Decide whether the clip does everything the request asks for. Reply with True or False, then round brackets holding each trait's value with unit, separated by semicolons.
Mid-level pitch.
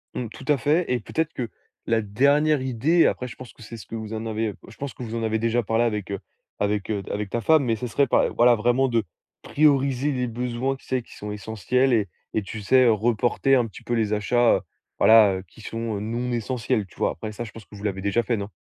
False (115 Hz)